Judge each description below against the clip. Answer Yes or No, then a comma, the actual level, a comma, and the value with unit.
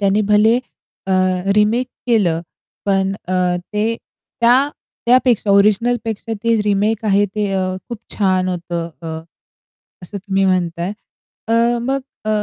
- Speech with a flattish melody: No, average, 3.1 semitones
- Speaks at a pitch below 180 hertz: No, high, 210 Hz